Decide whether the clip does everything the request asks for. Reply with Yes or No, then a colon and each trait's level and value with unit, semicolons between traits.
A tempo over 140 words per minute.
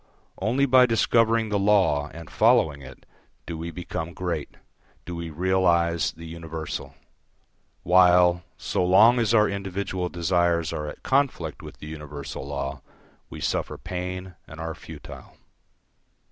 No: slow, 135 wpm